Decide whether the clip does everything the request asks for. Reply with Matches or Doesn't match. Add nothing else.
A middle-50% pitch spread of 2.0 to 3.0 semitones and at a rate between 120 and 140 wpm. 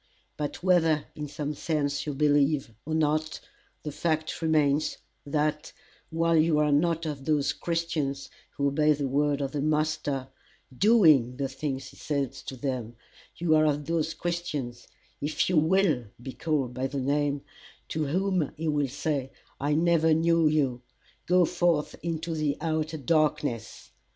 Doesn't match